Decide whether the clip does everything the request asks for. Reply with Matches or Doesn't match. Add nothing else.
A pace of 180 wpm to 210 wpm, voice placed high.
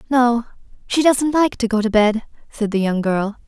Matches